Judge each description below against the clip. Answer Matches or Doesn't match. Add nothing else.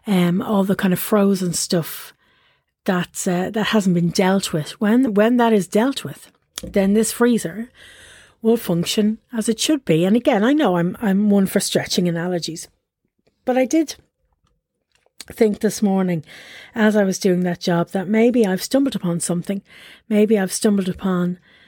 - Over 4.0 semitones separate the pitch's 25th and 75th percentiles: Doesn't match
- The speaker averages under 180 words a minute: Matches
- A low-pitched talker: Doesn't match